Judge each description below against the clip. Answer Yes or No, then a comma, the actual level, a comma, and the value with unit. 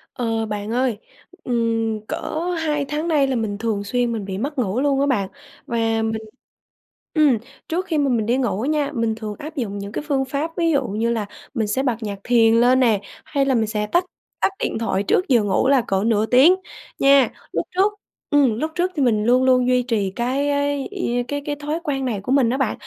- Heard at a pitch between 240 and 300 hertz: Yes, high, 245 Hz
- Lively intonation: No, average, 4.2 semitones